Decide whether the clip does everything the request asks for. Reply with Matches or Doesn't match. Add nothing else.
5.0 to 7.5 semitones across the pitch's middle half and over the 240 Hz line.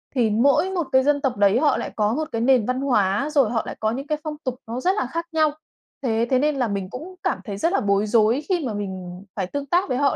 Matches